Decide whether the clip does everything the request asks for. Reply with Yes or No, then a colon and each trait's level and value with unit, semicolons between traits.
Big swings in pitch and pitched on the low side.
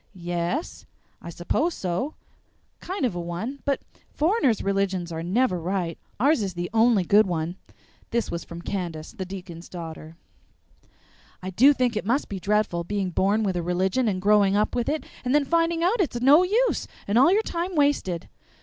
No: wide, 7.6 semitones; high, 200 Hz